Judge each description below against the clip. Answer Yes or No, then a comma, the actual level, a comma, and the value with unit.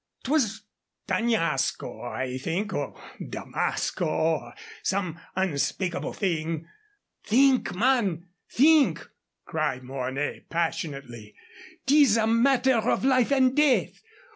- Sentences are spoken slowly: Yes, slow, 100 wpm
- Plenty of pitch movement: Yes, wide, 8.5 semitones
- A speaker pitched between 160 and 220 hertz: Yes, high, 190 Hz